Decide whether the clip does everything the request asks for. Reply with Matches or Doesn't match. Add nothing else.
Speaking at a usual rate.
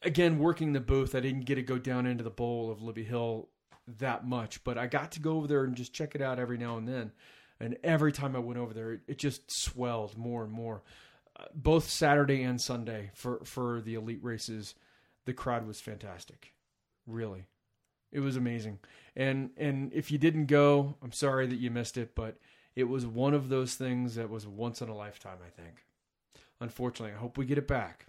Doesn't match